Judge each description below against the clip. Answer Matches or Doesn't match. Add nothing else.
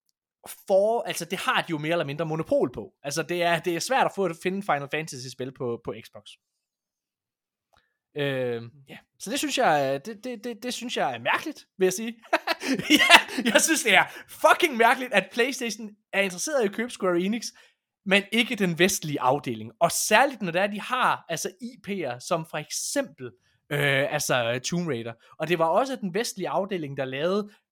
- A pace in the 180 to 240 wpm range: Matches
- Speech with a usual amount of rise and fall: Doesn't match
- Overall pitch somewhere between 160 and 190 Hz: Matches